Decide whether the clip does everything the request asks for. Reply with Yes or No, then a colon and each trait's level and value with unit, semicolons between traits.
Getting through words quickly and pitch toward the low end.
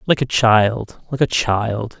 No: average, 180 wpm; low, 120 Hz